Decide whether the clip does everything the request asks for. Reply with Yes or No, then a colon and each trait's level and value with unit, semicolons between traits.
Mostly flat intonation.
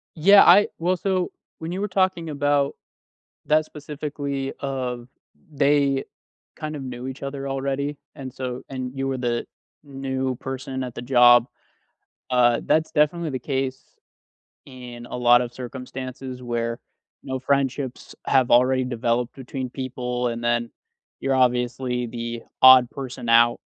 Yes: narrow, 2.3 semitones